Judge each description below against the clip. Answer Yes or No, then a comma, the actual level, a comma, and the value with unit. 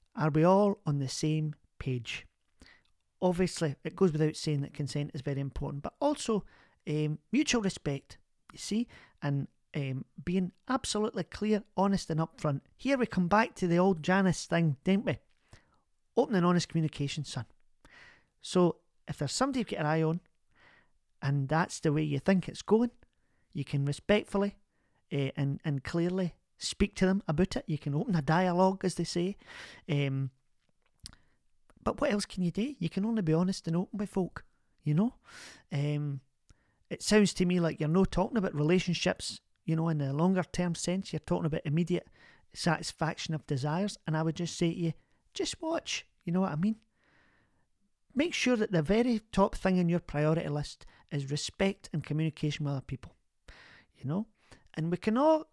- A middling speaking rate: Yes, average, 180 wpm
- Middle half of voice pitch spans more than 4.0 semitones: Yes, average, 4.7 semitones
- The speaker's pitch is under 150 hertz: No, medium, 170 Hz